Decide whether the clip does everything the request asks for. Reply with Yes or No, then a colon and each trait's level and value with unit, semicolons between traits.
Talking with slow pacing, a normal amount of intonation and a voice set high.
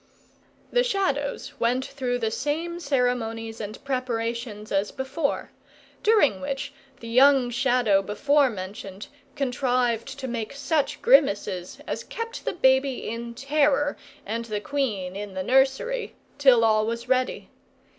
Yes: slow, 130 wpm; average, 3.9 semitones; very high, 250 Hz